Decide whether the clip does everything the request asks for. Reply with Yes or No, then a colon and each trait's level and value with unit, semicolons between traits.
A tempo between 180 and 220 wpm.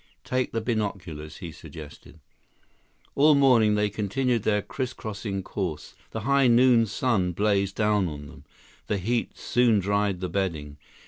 No: average, 140 wpm